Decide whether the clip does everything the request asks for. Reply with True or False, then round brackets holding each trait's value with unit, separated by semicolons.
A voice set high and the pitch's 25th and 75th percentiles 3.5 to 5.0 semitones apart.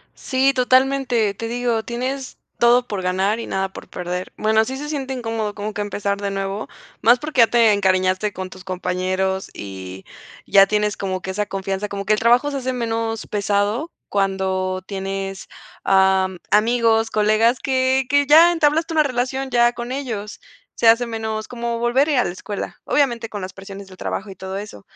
True (215 Hz; 4.1 semitones)